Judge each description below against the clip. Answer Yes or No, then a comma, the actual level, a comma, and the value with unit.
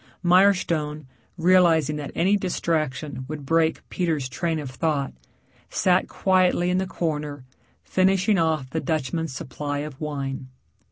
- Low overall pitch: No, medium, 160 Hz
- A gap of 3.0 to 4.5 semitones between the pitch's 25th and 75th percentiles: Yes, average, 3.8 semitones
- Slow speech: Yes, slow, 125 wpm